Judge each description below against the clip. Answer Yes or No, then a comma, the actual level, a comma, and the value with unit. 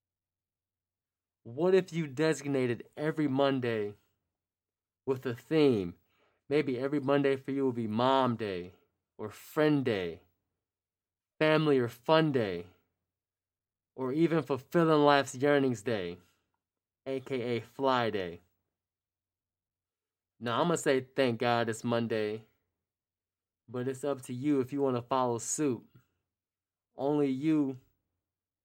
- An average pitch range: No, wide, 6.7 semitones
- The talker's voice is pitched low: Yes, low, 115 Hz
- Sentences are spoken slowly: Yes, slow, 115 wpm